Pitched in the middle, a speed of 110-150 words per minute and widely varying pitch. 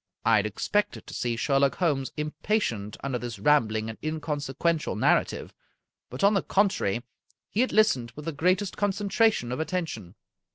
No: medium, 150 Hz; average, 160 wpm; wide, 7.9 semitones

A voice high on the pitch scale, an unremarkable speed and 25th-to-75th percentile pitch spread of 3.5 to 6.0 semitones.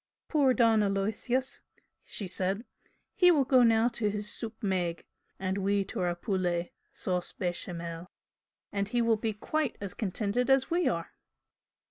Yes: high, 205 Hz; average, 150 wpm; average, 4.3 semitones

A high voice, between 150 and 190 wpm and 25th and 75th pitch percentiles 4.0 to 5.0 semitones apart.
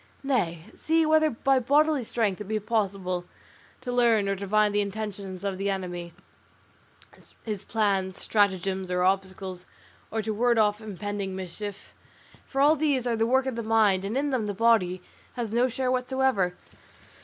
Yes: high, 210 Hz; average, 165 wpm; average, 4.3 semitones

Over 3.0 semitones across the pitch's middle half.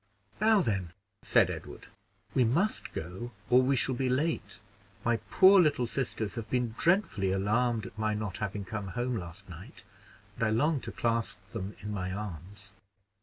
Yes: average, 4.1 semitones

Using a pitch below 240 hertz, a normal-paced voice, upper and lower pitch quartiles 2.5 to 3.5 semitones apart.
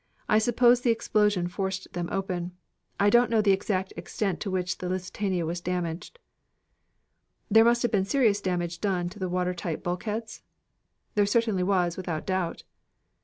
Yes: high, 190 Hz; average, 165 wpm; average, 3.2 semitones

